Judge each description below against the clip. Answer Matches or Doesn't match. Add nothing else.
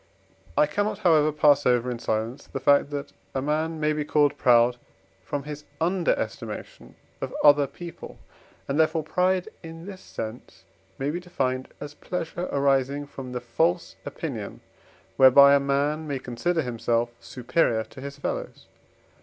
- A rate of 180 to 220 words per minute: Doesn't match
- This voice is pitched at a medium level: Matches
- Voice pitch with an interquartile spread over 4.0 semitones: Doesn't match